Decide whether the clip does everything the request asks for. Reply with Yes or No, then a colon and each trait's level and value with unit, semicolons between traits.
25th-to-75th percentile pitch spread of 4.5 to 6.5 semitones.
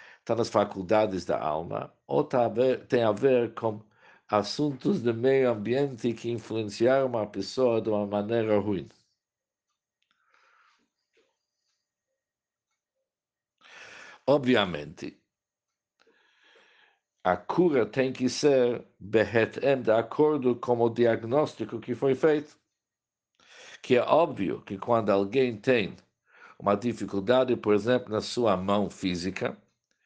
No: average, 3.9 semitones